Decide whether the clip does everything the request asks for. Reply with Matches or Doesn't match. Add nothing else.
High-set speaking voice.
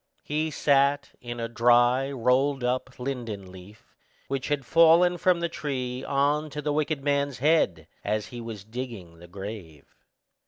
Doesn't match